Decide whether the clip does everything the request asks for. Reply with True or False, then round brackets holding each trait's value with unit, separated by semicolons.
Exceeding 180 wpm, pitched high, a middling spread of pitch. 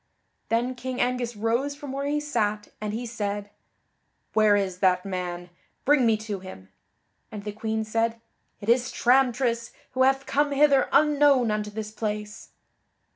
False (155 wpm; 230 Hz; 3.8 semitones)